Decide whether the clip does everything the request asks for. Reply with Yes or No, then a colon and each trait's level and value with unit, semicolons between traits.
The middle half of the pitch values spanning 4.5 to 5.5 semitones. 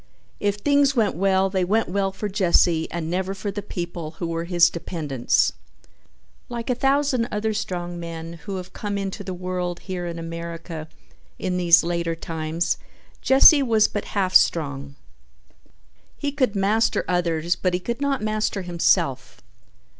No: average, 3.6 semitones